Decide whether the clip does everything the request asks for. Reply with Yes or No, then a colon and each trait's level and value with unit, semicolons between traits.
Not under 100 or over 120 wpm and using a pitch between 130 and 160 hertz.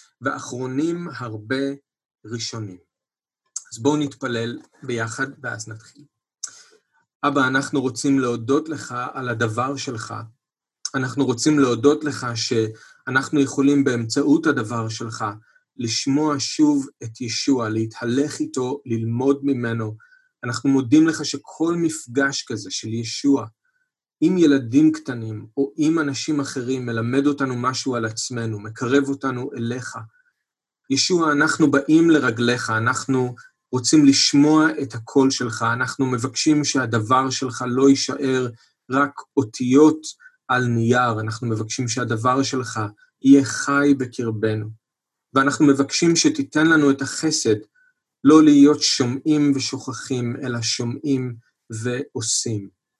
Yes: average, 110 wpm; low, 135 Hz